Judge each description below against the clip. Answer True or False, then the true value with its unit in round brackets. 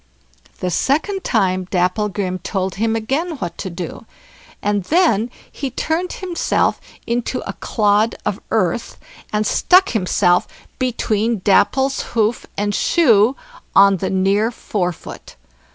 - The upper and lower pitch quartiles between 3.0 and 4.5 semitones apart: False (5.0 semitones)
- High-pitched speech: True (215 Hz)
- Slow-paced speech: True (120 wpm)